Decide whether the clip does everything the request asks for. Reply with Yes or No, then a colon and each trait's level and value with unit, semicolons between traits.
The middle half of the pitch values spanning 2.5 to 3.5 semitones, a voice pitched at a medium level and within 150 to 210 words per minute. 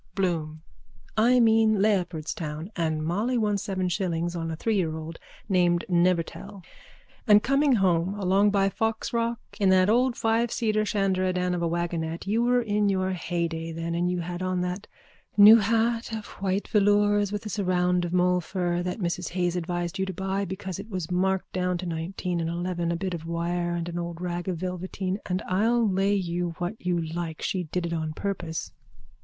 Yes: average, 2.9 semitones; medium, 180 Hz; average, 185 wpm